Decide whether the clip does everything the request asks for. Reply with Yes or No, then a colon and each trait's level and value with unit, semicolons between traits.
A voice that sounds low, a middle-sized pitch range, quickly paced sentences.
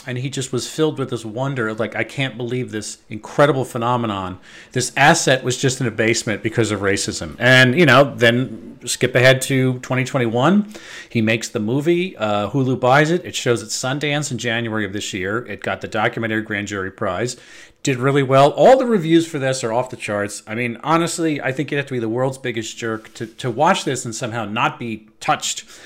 Yes: low, 125 Hz; average, 3.4 semitones; fast, 215 wpm